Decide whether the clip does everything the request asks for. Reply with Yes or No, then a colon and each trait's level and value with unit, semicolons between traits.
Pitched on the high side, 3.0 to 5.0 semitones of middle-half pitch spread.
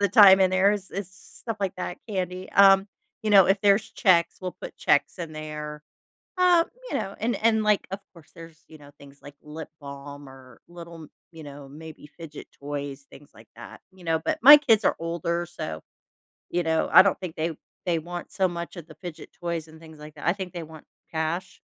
No: medium, 170 Hz; average, 4.0 semitones